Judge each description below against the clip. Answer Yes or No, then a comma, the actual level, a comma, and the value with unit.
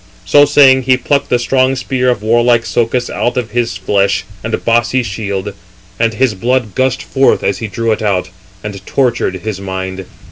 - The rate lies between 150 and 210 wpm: Yes, average, 180 wpm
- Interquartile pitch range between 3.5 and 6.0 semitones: Yes, average, 4.1 semitones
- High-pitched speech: No, low, 115 Hz